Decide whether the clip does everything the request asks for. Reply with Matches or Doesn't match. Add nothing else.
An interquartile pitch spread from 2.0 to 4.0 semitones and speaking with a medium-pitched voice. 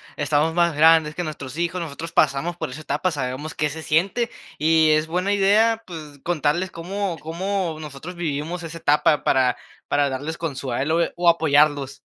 Matches